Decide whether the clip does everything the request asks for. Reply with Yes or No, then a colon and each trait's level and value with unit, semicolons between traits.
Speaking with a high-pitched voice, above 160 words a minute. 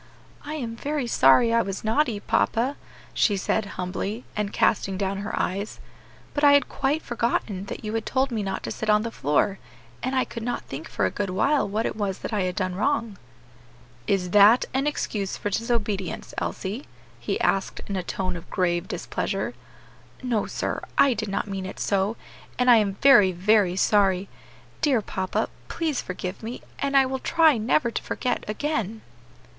Yes: high, 210 Hz; average, 185 wpm